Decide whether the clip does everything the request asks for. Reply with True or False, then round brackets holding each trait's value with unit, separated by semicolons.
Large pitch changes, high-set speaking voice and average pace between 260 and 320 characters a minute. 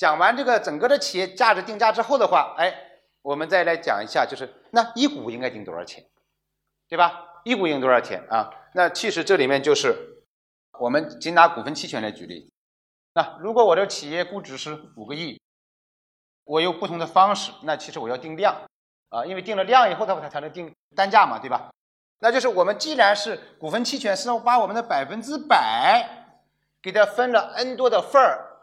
True (7.2 semitones; 200 Hz; 290 characters per minute)